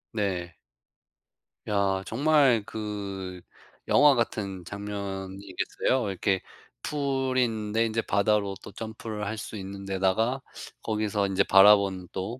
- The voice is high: No, low, 105 Hz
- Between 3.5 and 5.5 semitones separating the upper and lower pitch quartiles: No, narrow, 2.6 semitones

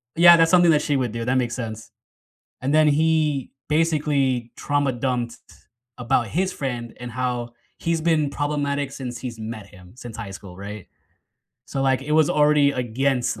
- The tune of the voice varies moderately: Yes, average, 4.0 semitones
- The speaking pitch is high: No, low, 135 Hz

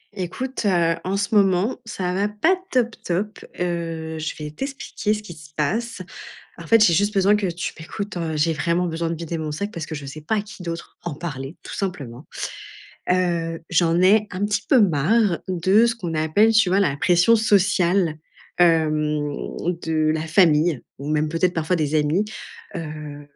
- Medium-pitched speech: Yes, medium, 175 Hz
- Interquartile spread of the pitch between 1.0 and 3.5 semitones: No, average, 4.3 semitones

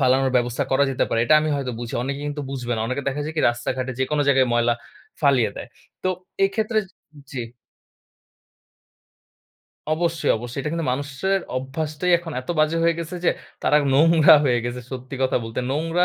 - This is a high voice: No, medium, 140 Hz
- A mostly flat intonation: No, average, 3.8 semitones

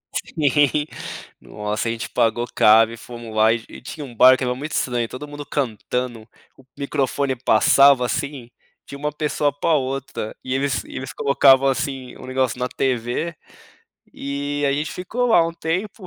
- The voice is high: No, low, 135 Hz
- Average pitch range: Yes, average, 3.1 semitones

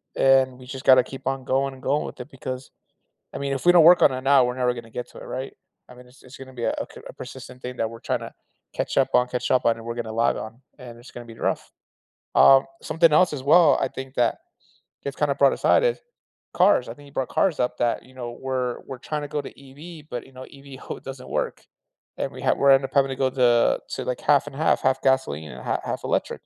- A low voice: Yes, low, 130 Hz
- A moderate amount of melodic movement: No, narrow, 1.9 semitones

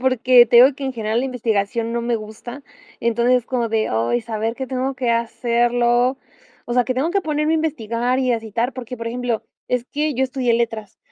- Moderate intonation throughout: No, narrow, 1.9 semitones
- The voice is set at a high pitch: Yes, high, 240 Hz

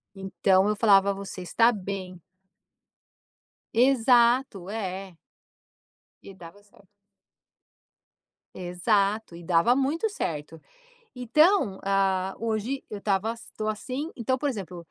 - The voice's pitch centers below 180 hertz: No, high, 200 Hz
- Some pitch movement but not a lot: Yes, average, 4.0 semitones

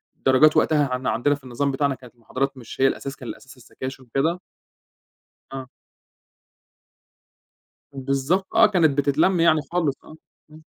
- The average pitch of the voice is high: No, medium, 140 Hz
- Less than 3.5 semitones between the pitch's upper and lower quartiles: Yes, average, 2.9 semitones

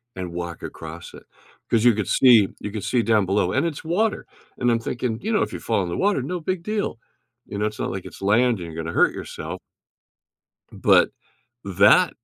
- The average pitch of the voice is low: Yes, low, 110 Hz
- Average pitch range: No, wide, 7.2 semitones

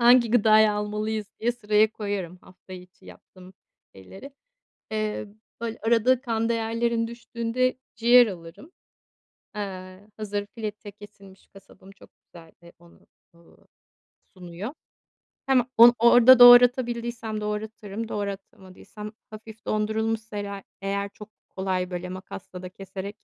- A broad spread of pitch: No, average, 3.0 semitones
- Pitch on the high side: Yes, high, 210 Hz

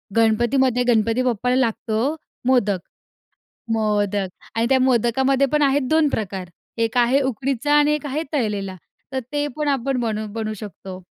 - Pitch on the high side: Yes, high, 240 Hz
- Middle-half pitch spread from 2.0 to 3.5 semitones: No, average, 3.9 semitones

